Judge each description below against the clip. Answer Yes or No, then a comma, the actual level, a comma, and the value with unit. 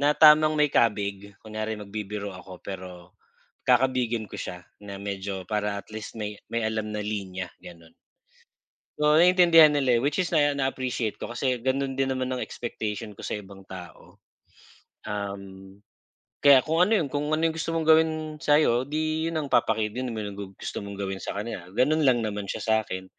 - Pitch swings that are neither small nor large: No, wide, 6.1 semitones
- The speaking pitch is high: No, low, 110 Hz